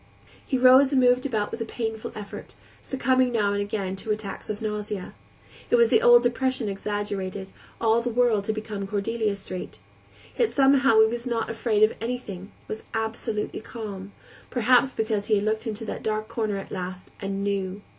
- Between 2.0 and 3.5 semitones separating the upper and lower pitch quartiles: Yes, average, 3.1 semitones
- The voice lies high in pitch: Yes, high, 220 Hz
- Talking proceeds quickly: No, average, 180 wpm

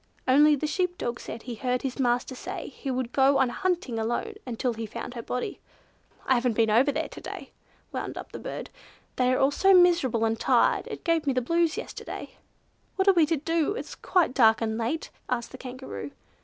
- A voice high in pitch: Yes, very high, 260 Hz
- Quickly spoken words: Yes, fast, 215 wpm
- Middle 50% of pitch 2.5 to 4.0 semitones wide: No, average, 5.2 semitones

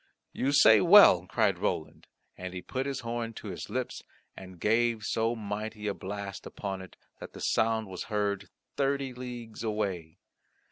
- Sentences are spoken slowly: No, average, 160 wpm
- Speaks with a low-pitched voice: Yes, low, 110 Hz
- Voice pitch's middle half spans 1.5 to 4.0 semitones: Yes, average, 3.1 semitones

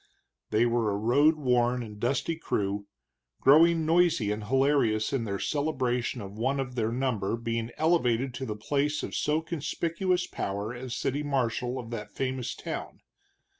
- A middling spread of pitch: Yes, average, 4.4 semitones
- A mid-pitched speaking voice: No, low, 125 Hz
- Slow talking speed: No, average, 160 wpm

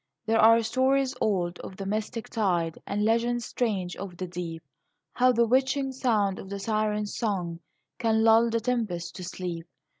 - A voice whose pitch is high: Yes, high, 215 Hz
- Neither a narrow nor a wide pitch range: Yes, average, 4.1 semitones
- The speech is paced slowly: No, average, 170 wpm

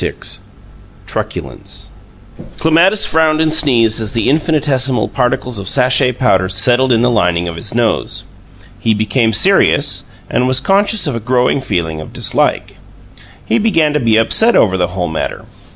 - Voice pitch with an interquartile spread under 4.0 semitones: No, wide, 5.5 semitones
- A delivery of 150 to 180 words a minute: Yes, average, 155 wpm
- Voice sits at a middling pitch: No, low, 125 Hz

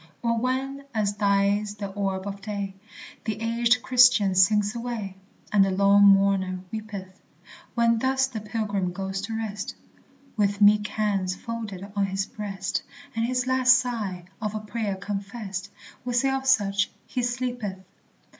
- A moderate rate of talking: Yes, average, 145 wpm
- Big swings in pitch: No, average, 3.0 semitones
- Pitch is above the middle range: Yes, high, 210 Hz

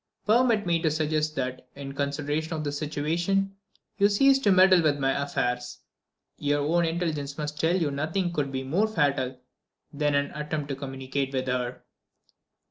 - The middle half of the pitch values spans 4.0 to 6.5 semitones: No, average, 3.6 semitones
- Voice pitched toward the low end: No, medium, 150 Hz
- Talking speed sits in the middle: Yes, average, 165 wpm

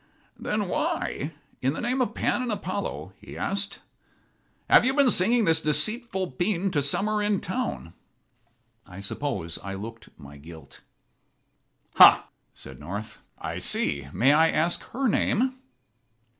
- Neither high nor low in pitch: Yes, medium, 165 Hz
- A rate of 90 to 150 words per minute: Yes, average, 140 wpm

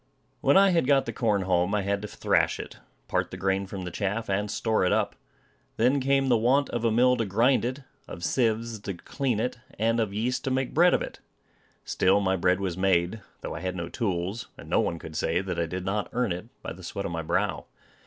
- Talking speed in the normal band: No, fast, 240 wpm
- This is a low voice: Yes, low, 105 Hz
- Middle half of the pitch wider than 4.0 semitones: Yes, average, 4.5 semitones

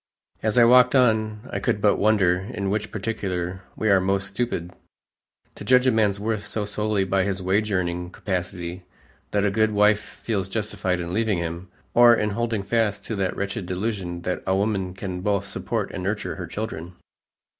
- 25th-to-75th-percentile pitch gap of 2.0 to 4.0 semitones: Yes, average, 2.8 semitones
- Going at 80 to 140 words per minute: No, average, 185 wpm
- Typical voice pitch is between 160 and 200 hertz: No, low, 100 Hz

